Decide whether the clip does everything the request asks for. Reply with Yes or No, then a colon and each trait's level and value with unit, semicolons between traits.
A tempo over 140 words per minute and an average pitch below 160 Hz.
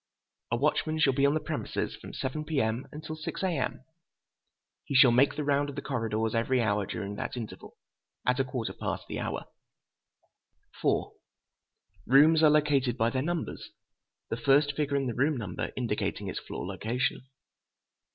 Yes: average, 160 wpm; low, 135 Hz